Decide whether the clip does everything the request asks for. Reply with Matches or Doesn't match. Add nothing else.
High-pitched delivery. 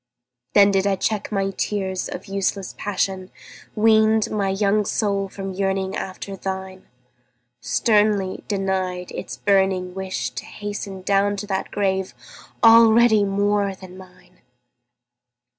Matches